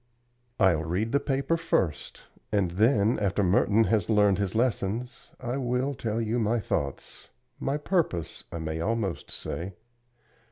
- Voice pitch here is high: No, low, 110 Hz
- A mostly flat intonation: No, average, 4.4 semitones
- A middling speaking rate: Yes, average, 145 wpm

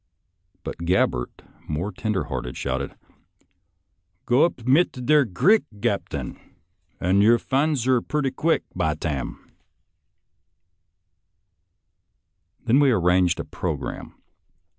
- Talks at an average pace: No, slow, 110 wpm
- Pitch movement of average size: No, wide, 7.3 semitones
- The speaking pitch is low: Yes, very low, 95 Hz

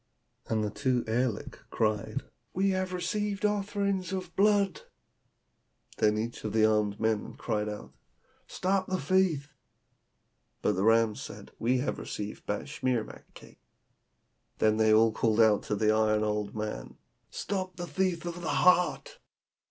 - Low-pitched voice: Yes, low, 120 Hz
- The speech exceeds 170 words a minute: No, average, 145 wpm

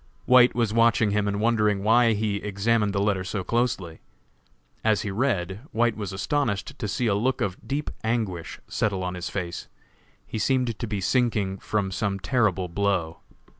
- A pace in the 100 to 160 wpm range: No, average, 170 wpm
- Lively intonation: No, average, 3.2 semitones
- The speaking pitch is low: Yes, low, 105 Hz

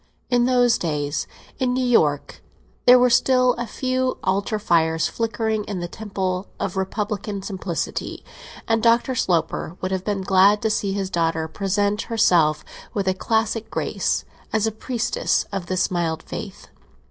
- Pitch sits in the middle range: No, high, 200 Hz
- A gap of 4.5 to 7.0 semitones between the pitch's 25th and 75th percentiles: No, average, 3.8 semitones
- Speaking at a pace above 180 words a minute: No, average, 155 wpm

